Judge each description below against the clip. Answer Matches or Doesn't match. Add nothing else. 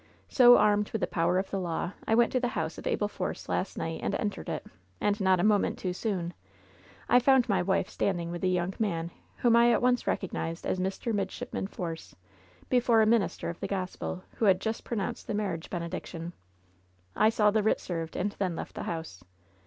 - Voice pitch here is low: Doesn't match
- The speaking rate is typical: Doesn't match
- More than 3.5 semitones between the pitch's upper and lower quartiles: Matches